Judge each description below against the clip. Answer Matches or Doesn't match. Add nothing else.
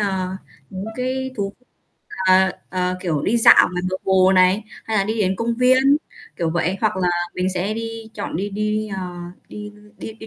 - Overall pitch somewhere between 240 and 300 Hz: Doesn't match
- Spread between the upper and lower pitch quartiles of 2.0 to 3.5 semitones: Matches